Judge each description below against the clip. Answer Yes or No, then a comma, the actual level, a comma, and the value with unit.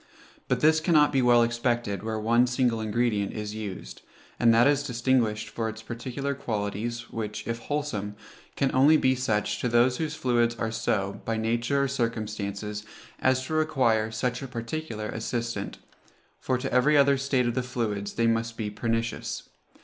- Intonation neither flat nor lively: Yes, average, 3.0 semitones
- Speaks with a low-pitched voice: Yes, low, 120 Hz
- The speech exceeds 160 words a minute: Yes, average, 170 wpm